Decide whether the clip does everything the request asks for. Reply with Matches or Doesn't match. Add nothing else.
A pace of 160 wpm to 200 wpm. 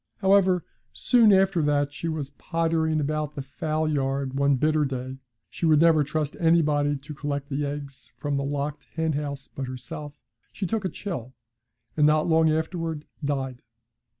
Matches